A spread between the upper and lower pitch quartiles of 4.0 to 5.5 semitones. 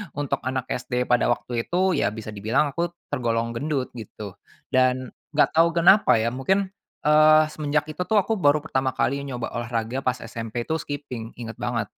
Yes: average, 4.6 semitones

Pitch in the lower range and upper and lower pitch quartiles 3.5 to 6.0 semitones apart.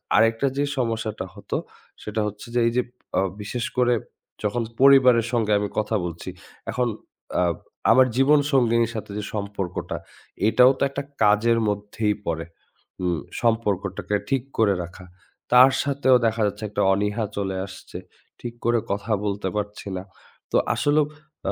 No: low, 110 Hz; average, 3.1 semitones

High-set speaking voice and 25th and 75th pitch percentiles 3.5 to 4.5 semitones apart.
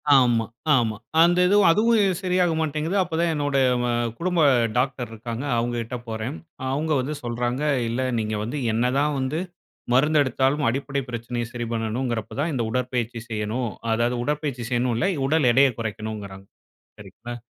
No: low, 125 Hz; average, 4.2 semitones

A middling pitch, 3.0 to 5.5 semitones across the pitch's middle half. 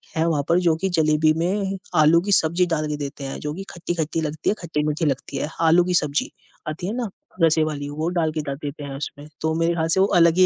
No: medium, 160 Hz; narrow, 2.6 semitones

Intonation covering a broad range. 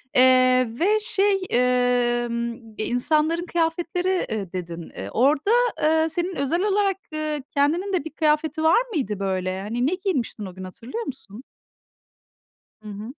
Yes: wide, 7.0 semitones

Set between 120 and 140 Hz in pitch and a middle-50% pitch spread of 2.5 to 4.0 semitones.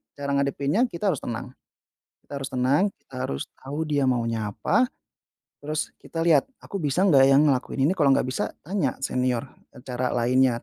Yes: low, 135 Hz; average, 3.0 semitones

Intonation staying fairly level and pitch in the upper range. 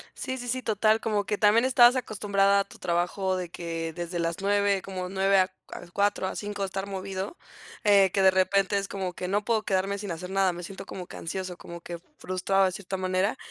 Yes: narrow, 1.7 semitones; high, 195 Hz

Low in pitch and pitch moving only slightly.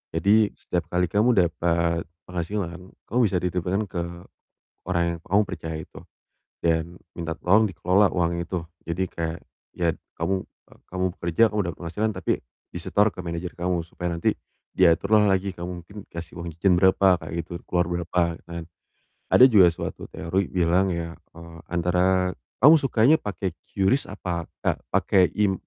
Yes: very low, 90 Hz; narrow, 2.3 semitones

